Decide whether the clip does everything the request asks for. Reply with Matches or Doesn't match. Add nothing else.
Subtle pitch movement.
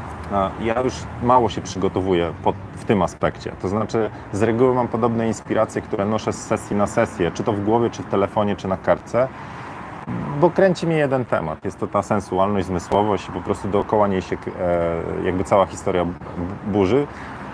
Doesn't match